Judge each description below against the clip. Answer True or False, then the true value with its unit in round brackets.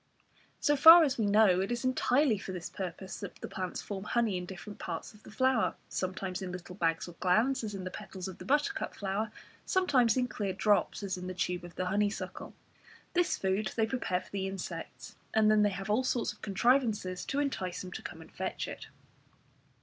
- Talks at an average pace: False (210 wpm)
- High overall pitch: True (200 Hz)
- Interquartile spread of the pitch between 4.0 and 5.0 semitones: True (4.3 semitones)